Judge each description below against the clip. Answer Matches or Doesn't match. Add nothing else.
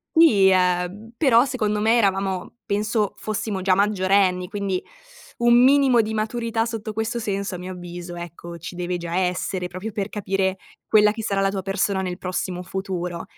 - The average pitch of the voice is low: Doesn't match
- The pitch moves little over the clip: Doesn't match